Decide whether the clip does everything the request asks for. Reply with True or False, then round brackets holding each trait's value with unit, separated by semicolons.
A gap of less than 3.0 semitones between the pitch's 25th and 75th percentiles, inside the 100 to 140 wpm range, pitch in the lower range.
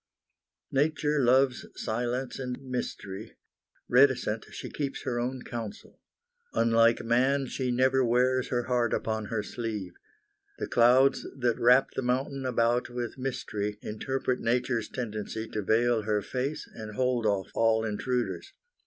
True (2.4 semitones; 135 wpm; 120 Hz)